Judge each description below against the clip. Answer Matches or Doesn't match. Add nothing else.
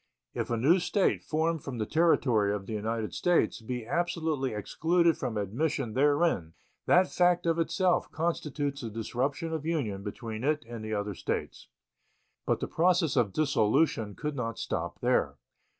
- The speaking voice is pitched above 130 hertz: Matches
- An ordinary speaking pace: Matches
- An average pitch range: Doesn't match